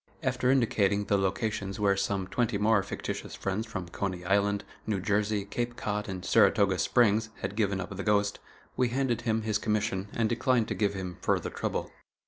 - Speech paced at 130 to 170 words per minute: No, average, 180 wpm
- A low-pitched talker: Yes, low, 105 Hz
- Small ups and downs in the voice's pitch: Yes, narrow, 2.3 semitones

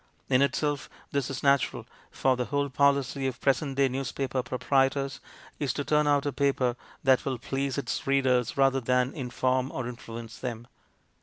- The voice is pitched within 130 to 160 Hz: Yes, low, 135 Hz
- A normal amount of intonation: No, narrow, 1.7 semitones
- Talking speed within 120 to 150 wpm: No, average, 170 wpm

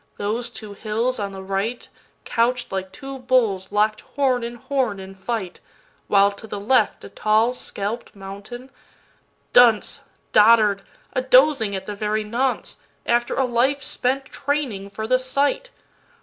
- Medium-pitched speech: No, high, 230 Hz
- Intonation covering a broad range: No, average, 4.0 semitones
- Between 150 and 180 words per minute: No, slow, 135 wpm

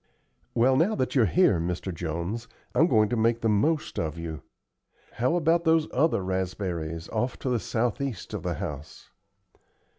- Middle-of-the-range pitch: No, low, 110 Hz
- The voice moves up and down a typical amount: No, wide, 7.3 semitones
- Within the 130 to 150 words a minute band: No, average, 160 wpm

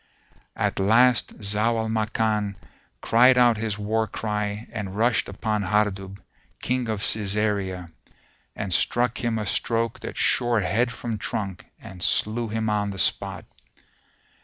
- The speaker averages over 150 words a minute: No, slow, 135 wpm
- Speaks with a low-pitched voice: Yes, low, 110 Hz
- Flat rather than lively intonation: Yes, narrow, 2.0 semitones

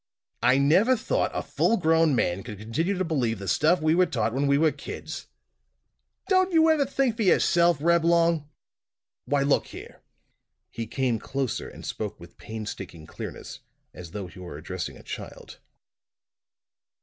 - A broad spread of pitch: Yes, wide, 7.9 semitones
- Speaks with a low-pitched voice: No, medium, 145 Hz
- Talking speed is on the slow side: No, average, 160 wpm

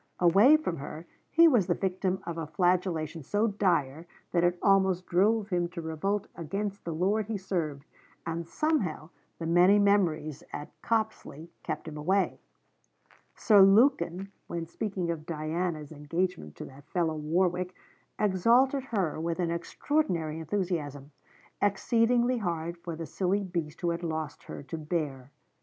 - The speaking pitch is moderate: Yes, medium, 175 Hz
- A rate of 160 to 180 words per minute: No, average, 150 wpm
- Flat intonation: No, average, 3.7 semitones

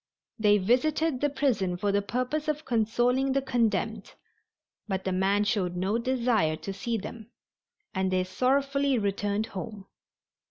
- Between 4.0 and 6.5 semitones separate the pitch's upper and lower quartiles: Yes, average, 4.8 semitones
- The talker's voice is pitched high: Yes, high, 220 Hz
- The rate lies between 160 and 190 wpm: No, average, 145 wpm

